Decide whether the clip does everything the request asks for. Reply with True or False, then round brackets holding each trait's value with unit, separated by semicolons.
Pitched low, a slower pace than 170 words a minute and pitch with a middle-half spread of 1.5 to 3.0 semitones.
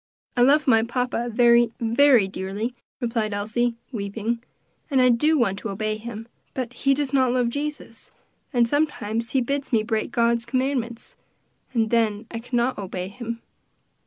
False (235 Hz; 160 wpm; 2.4 semitones)